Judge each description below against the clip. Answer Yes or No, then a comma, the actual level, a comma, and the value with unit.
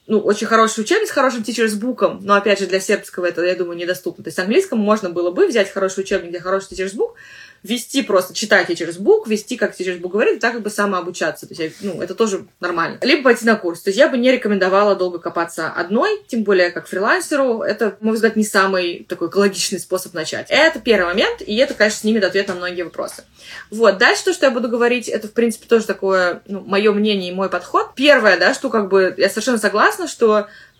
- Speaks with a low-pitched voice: No, high, 205 Hz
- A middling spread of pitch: Yes, average, 3.9 semitones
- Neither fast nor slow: No, fast, 230 wpm